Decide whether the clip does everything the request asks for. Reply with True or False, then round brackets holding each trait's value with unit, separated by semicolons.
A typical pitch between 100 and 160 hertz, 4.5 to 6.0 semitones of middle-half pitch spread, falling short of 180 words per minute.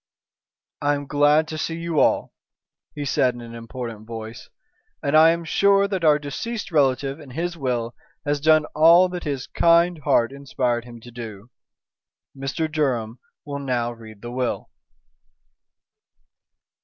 True (140 Hz; 4.8 semitones; 150 wpm)